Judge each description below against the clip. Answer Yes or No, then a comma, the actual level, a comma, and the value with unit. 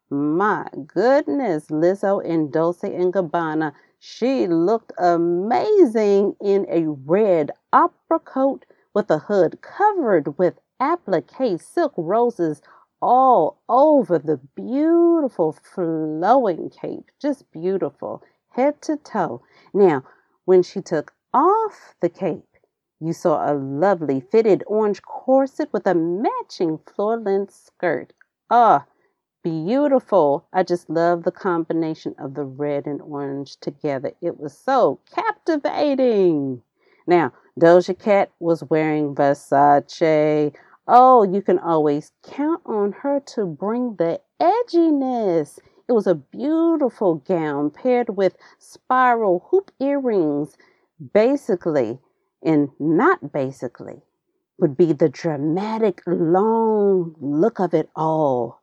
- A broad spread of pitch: Yes, wide, 8.3 semitones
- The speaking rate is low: Yes, slow, 115 wpm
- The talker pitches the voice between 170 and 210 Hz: Yes, medium, 185 Hz